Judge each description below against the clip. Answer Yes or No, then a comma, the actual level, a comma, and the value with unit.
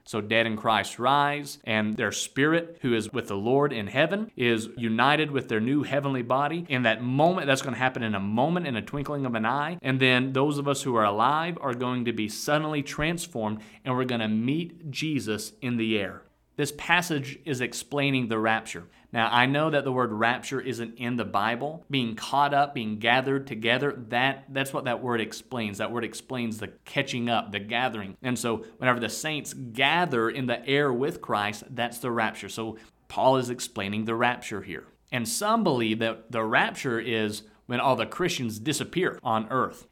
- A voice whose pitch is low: Yes, low, 125 Hz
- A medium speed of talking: Yes, average, 195 wpm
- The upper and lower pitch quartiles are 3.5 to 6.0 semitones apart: Yes, average, 4.0 semitones